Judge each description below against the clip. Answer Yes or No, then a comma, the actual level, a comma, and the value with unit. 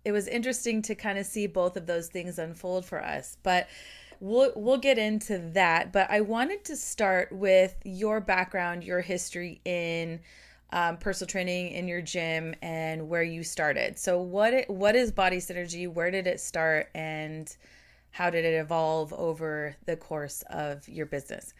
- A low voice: No, medium, 180 Hz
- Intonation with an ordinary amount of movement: Yes, average, 3.2 semitones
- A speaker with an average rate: Yes, average, 175 wpm